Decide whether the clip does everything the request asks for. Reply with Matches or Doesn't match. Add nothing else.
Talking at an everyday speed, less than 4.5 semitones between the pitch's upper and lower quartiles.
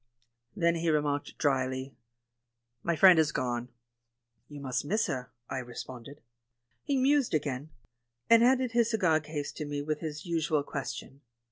Matches